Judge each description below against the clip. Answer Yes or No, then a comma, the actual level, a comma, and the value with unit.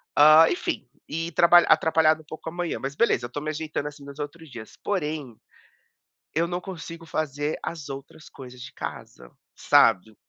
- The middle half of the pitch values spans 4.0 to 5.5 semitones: No, average, 2.8 semitones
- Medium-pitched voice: Yes, medium, 155 Hz